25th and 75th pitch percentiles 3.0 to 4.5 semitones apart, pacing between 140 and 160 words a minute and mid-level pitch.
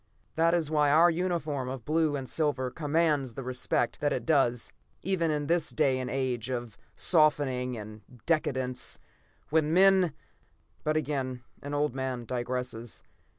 Yes: average, 3.7 semitones; average, 150 wpm; medium, 145 Hz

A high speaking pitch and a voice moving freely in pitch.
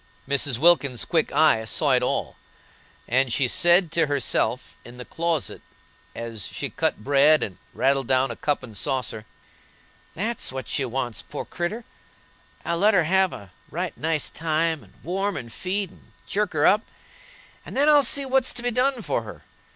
No: medium, 155 Hz; wide, 6.4 semitones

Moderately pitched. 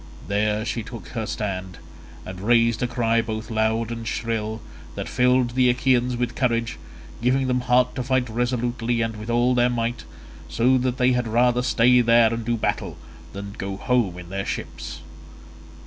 No: low, 115 Hz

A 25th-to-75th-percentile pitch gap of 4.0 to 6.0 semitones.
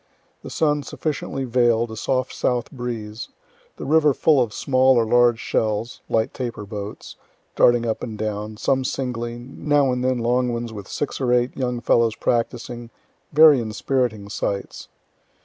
No: narrow, 2.6 semitones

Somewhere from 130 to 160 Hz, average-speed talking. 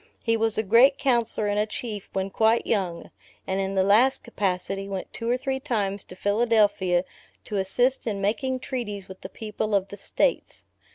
No: high, 210 Hz; average, 185 wpm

